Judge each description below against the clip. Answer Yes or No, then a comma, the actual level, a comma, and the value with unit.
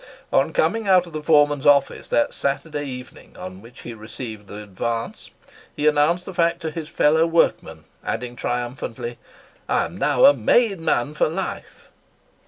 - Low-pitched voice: No, medium, 145 Hz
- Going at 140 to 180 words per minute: Yes, average, 165 wpm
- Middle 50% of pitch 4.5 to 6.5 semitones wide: Yes, wide, 5.5 semitones